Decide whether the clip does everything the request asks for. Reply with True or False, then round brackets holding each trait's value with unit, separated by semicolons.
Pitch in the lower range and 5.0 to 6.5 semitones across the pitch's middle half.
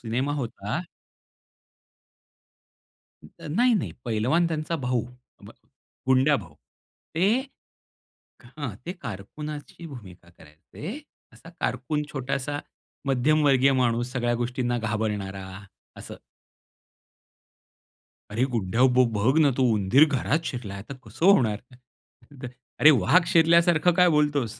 True (130 Hz; 5.3 semitones)